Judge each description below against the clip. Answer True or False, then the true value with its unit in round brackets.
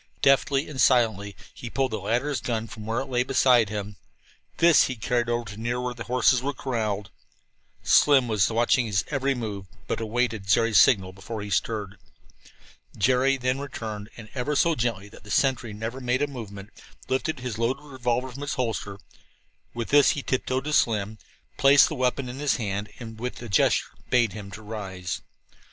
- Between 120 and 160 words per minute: False (180 wpm)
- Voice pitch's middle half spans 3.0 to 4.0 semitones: True (3.5 semitones)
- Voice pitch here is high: False (120 Hz)